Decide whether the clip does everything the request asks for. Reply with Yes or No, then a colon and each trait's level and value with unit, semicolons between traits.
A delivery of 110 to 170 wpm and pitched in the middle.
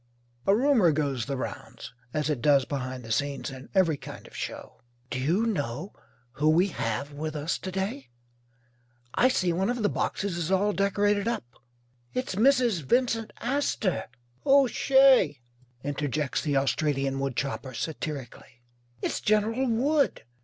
Yes: average, 145 wpm; medium, 165 Hz